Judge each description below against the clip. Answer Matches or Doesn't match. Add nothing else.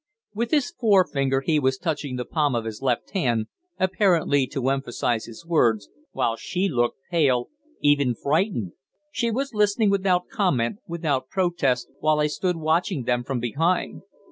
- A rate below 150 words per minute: Doesn't match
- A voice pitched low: Doesn't match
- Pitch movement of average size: Doesn't match